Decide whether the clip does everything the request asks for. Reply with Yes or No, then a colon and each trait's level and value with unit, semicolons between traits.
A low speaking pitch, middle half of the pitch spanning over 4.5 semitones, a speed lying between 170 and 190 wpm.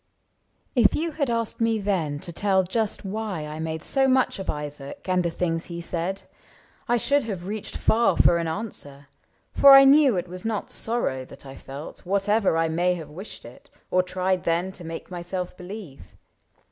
No: medium, 185 Hz; average, 5.0 semitones; average, 185 wpm